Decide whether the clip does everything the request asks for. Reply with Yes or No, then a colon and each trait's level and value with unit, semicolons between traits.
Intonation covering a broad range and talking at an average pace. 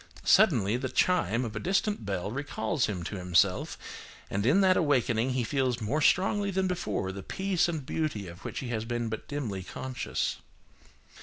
Yes: wide, 7.4 semitones; average, 175 wpm